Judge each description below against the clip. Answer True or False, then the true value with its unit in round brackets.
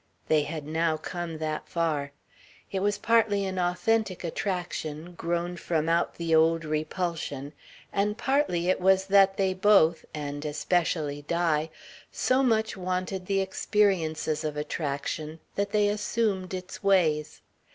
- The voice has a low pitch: False (175 Hz)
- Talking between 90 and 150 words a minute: True (135 wpm)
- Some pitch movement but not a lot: True (3.8 semitones)